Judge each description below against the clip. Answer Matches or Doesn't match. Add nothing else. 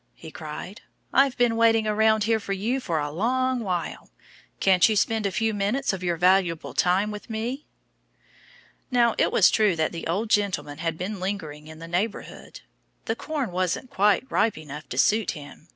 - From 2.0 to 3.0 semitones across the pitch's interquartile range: Doesn't match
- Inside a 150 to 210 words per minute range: Matches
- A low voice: Doesn't match